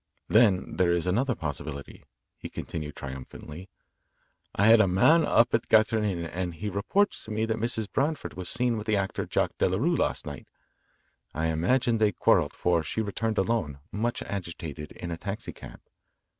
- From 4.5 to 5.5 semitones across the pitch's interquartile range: Yes, average, 4.9 semitones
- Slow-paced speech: No, average, 175 wpm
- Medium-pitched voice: No, low, 100 Hz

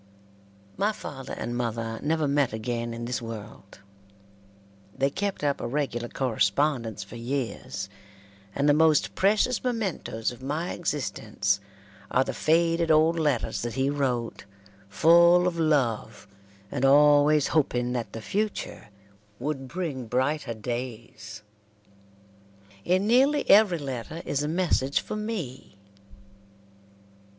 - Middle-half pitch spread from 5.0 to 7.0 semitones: Yes, wide, 5.6 semitones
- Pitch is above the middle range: No, medium, 140 Hz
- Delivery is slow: Yes, slow, 125 wpm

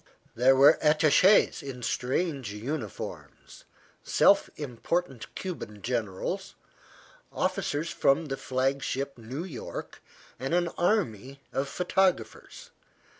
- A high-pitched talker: No, medium, 140 Hz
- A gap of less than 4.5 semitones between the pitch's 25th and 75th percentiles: No, average, 5.1 semitones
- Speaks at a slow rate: Yes, slow, 95 wpm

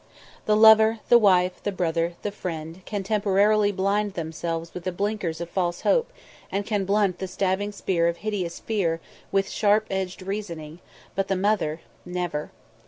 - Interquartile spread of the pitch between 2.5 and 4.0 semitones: Yes, average, 3.2 semitones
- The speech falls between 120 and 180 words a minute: Yes, average, 165 wpm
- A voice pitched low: No, high, 190 Hz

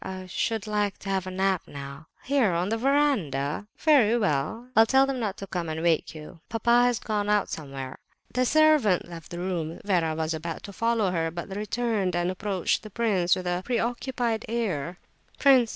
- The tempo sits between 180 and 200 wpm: Yes, average, 195 wpm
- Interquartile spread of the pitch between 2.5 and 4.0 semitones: No, wide, 5.4 semitones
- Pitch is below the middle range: No, high, 195 Hz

